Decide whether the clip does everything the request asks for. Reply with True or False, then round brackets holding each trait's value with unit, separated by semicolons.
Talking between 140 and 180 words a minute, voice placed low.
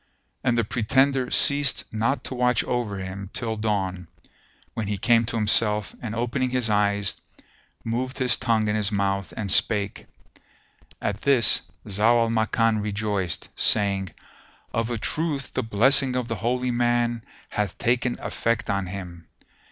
True (150 wpm; 115 Hz)